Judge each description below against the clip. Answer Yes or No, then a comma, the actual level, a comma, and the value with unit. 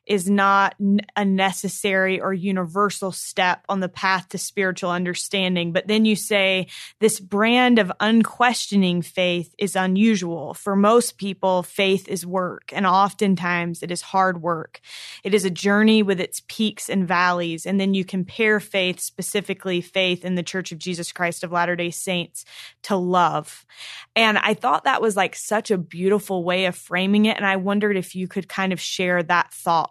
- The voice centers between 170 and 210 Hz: Yes, high, 190 Hz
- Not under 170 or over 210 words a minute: Yes, average, 175 wpm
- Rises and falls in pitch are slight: Yes, narrow, 2.2 semitones